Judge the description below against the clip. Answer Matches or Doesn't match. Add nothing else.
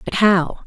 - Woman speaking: Matches